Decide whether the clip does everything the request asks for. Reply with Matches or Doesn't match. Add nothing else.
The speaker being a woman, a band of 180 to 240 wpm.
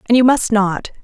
Matches